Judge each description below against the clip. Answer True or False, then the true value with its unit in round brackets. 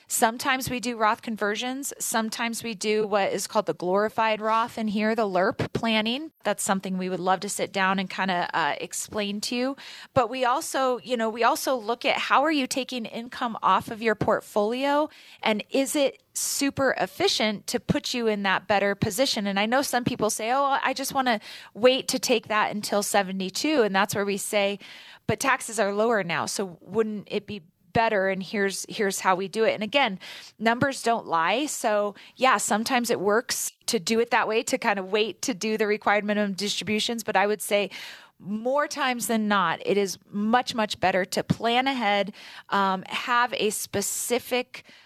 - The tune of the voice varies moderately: True (3.3 semitones)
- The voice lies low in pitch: False (220 Hz)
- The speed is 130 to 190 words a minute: False (200 wpm)